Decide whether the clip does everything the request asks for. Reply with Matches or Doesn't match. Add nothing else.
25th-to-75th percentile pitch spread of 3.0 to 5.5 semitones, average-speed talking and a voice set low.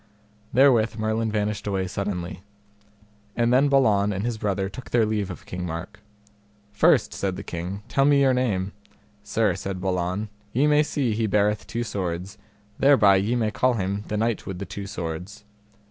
Matches